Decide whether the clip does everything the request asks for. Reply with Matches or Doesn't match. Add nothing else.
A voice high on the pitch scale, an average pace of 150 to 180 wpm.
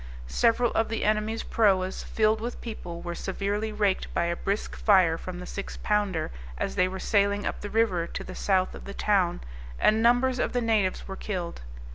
Doesn't match